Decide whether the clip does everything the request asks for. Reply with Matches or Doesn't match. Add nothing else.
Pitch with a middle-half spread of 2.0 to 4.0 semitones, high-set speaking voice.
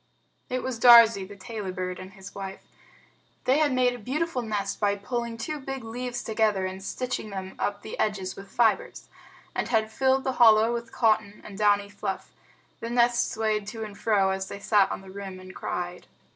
Matches